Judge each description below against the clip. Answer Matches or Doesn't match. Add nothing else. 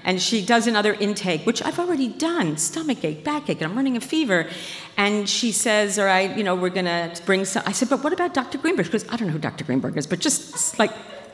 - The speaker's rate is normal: Doesn't match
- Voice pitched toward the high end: Matches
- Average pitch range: Doesn't match